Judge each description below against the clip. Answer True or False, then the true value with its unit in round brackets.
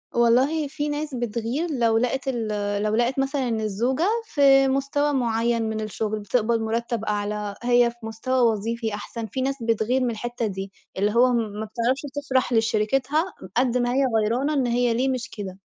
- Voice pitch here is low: False (235 Hz)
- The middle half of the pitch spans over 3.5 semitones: False (3.2 semitones)